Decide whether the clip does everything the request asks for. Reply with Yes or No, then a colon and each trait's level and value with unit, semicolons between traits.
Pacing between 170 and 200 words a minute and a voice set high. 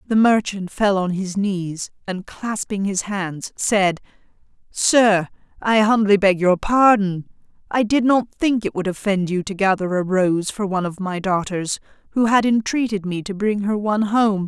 Yes: average, 180 wpm; high, 200 Hz